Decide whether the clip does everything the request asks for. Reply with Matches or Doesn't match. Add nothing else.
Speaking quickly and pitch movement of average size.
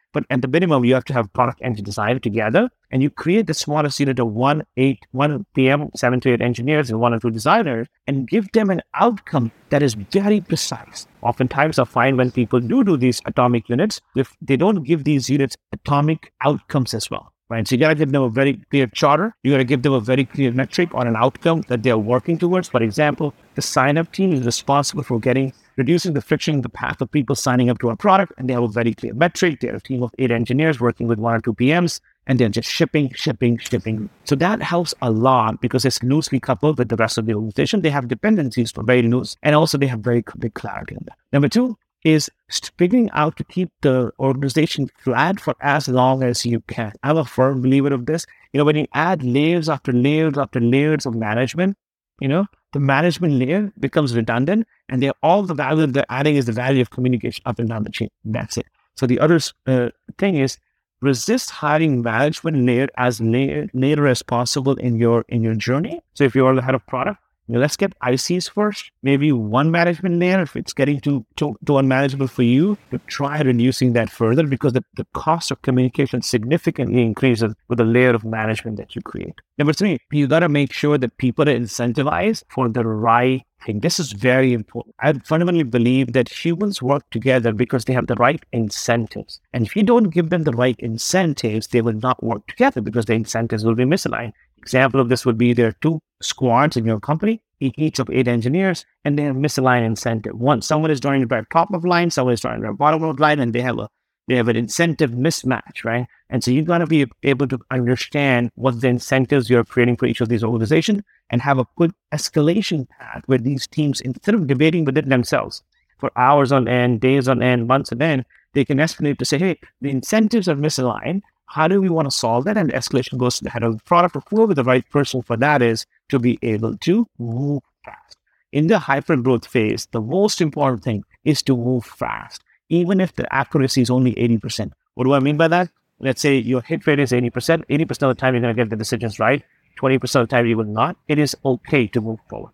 Matches